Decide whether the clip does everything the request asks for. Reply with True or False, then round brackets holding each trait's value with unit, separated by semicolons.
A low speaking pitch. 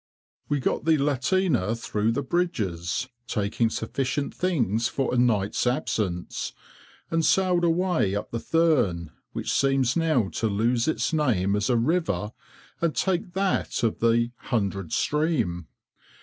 True (125 Hz)